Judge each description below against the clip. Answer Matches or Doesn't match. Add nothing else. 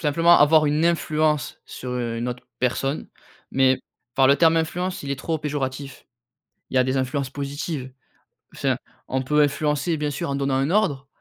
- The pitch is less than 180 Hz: Matches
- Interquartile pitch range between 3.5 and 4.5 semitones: Doesn't match